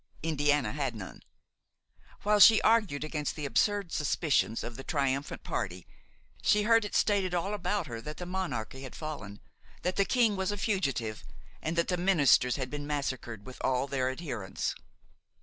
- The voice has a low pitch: No, medium, 150 Hz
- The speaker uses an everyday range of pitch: No, wide, 6.5 semitones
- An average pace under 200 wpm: Yes, average, 165 wpm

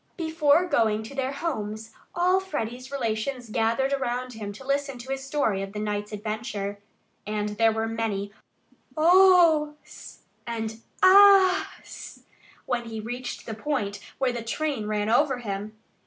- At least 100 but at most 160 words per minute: Yes, average, 140 wpm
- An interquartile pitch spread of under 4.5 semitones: No, average, 5.1 semitones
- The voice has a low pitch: No, high, 240 Hz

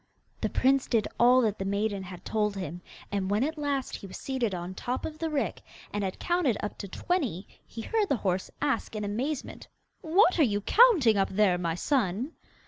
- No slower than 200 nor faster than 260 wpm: Yes, fast, 205 wpm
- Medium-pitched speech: No, high, 220 Hz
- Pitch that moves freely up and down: Yes, wide, 6.4 semitones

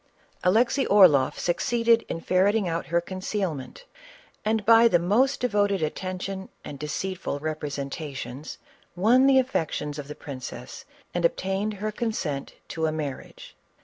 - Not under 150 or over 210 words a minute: No, slow, 135 wpm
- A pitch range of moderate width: No, wide, 5.9 semitones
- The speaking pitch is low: No, medium, 185 Hz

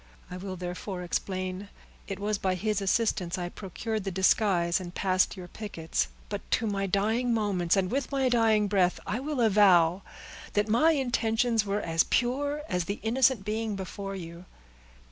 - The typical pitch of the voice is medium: No, high, 200 Hz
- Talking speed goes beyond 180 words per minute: No, average, 170 wpm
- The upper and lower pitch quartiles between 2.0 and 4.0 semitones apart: Yes, average, 3.4 semitones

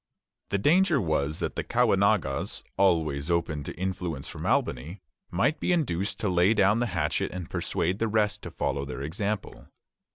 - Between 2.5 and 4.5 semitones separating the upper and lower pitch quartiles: No, average, 4.9 semitones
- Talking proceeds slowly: No, average, 165 wpm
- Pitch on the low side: Yes, very low, 95 Hz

